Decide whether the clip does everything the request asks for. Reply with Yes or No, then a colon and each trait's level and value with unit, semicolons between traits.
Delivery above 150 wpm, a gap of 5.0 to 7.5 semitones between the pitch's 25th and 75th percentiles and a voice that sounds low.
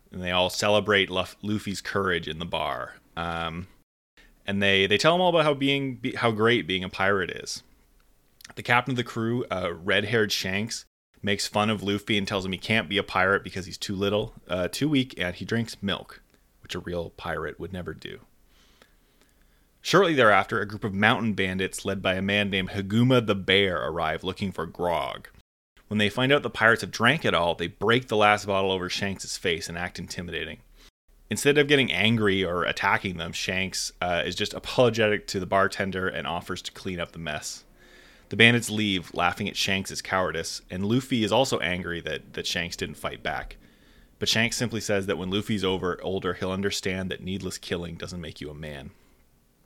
No: average, 195 wpm; average, 3.1 semitones; low, 100 Hz